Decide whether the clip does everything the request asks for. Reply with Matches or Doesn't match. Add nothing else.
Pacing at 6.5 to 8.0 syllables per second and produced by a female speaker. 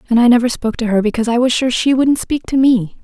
Matches